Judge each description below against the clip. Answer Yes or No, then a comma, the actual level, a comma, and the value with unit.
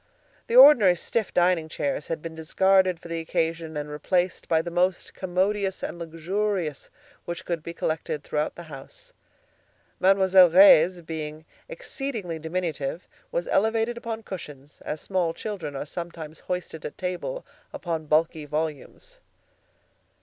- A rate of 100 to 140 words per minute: Yes, slow, 135 wpm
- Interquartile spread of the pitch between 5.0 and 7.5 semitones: No, average, 3.3 semitones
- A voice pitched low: No, medium, 170 Hz